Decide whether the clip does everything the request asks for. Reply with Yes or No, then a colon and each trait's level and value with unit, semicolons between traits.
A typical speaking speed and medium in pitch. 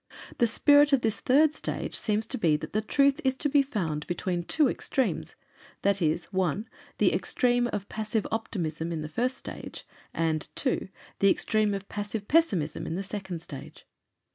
No: average, 175 wpm; high, 210 Hz